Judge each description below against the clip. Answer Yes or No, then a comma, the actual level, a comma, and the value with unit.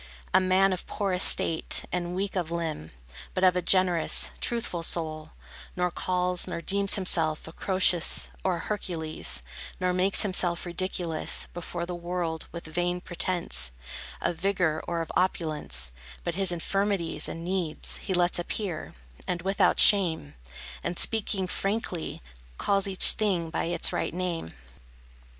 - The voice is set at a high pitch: No, medium, 180 Hz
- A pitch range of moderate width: No, narrow, 2.2 semitones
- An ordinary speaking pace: Yes, average, 145 wpm